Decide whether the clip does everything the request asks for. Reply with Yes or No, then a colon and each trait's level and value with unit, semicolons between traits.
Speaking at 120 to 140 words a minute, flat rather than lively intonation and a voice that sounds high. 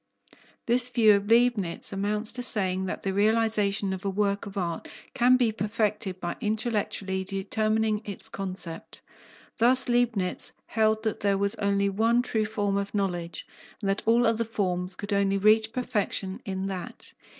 No: average, 160 wpm; narrow, 2.3 semitones; high, 205 Hz